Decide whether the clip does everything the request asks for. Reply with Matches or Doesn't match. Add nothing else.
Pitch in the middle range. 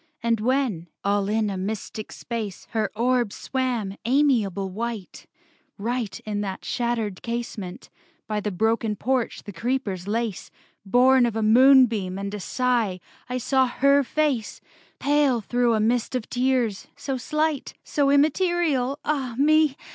Doesn't match